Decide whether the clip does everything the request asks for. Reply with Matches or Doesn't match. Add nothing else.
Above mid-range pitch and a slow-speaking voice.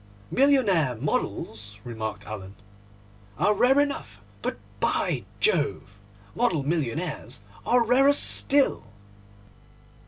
Doesn't match